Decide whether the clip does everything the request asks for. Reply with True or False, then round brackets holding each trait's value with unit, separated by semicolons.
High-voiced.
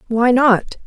True (235 Hz)